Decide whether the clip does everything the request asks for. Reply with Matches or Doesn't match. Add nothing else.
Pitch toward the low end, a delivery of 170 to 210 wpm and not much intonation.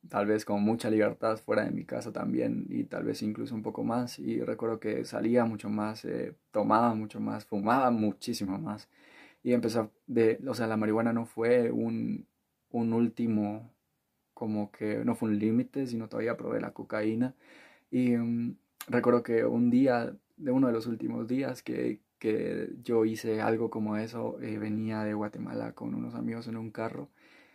Matches